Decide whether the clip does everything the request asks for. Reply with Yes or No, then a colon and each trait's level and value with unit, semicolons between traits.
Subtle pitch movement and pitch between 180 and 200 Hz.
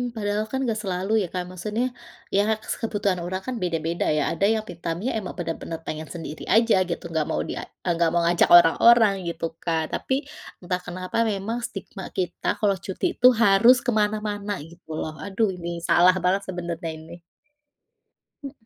No: average, 3.8 semitones; high, 190 Hz